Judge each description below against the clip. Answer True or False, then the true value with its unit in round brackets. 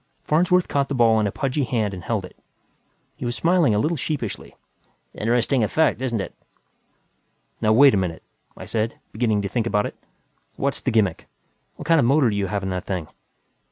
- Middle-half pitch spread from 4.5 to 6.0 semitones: True (5.2 semitones)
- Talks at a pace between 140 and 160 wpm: False (195 wpm)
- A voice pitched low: True (115 Hz)